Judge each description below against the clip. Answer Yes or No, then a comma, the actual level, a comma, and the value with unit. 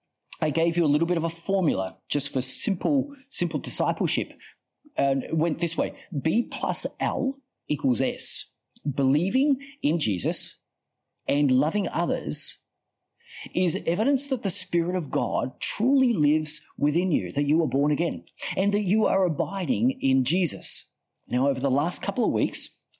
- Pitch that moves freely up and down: Yes, wide, 6.7 semitones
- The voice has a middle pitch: Yes, medium, 170 Hz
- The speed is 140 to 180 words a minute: Yes, average, 155 wpm